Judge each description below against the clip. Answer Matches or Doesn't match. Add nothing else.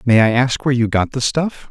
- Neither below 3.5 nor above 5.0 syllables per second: Doesn't match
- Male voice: Matches